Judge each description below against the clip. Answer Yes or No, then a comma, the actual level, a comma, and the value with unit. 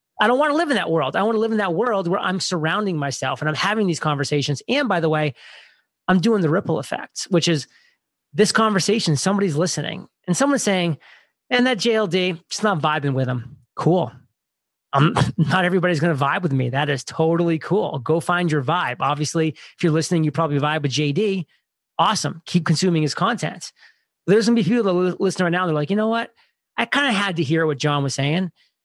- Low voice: No, medium, 170 Hz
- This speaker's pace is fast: Yes, fast, 215 wpm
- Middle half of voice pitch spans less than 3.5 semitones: No, average, 4.7 semitones